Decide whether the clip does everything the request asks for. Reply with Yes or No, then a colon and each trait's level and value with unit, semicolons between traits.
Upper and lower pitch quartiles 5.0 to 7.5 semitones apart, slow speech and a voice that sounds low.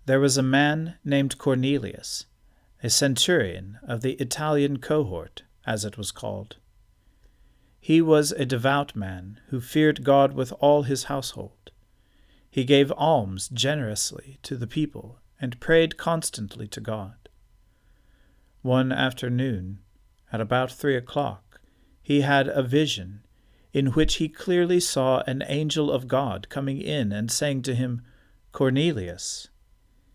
Yes: average, 5.3 semitones; slow, 130 wpm; low, 130 Hz